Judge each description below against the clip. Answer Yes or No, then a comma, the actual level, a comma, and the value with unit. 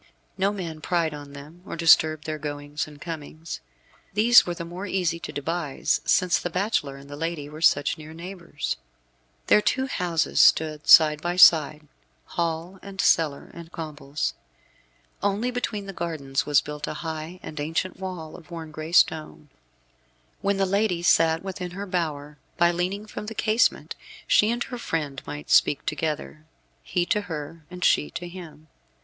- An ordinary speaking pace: Yes, average, 165 wpm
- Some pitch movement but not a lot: Yes, average, 3.3 semitones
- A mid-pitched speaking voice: Yes, medium, 165 Hz